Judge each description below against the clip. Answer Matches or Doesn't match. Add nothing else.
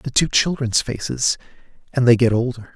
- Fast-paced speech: Doesn't match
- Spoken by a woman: Doesn't match